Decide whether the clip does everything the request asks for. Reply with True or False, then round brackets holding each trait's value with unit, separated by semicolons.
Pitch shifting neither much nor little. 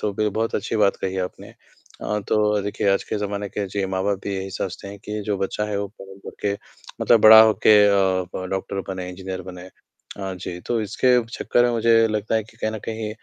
False (2.1 semitones)